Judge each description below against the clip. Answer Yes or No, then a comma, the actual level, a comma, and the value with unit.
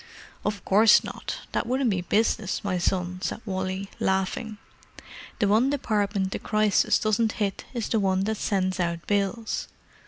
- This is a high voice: Yes, high, 200 Hz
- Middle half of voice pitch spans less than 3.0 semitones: Yes, narrow, 2.6 semitones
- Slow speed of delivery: No, average, 150 wpm